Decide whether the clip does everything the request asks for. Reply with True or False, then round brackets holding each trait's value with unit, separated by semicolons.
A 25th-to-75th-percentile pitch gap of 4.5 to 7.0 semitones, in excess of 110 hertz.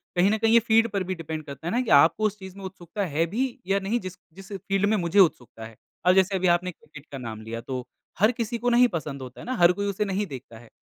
True (5.2 semitones; 185 Hz)